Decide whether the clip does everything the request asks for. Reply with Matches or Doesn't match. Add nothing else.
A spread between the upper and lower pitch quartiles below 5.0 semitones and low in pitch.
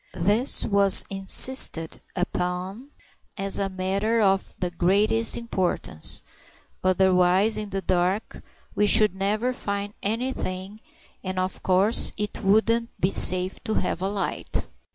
Doesn't match